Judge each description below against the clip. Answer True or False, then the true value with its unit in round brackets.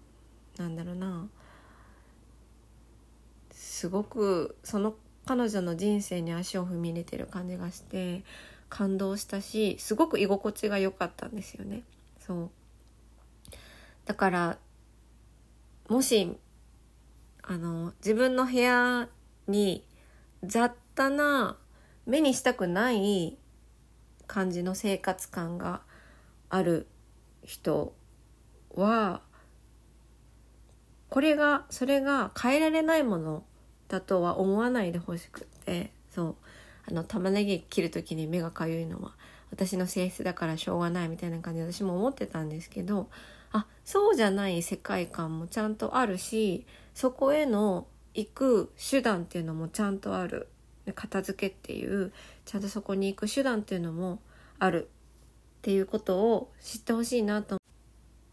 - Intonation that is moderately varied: True (4.2 semitones)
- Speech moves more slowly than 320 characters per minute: True (250 characters per minute)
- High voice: True (195 Hz)